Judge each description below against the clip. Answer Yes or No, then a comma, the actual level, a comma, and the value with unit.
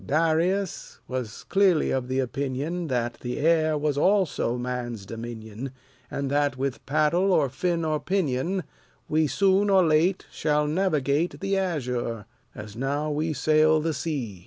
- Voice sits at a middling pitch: Yes, medium, 150 Hz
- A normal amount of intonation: Yes, average, 4.7 semitones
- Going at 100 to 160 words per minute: Yes, average, 145 wpm